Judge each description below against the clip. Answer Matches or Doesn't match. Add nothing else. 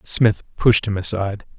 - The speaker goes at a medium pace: Matches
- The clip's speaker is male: Matches